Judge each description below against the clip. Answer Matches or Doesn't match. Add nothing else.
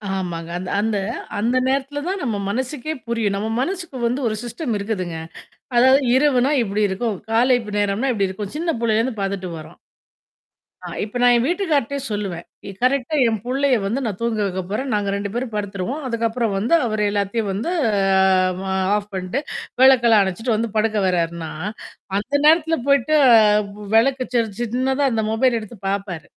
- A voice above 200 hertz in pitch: Matches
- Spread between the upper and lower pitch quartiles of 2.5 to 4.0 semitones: Doesn't match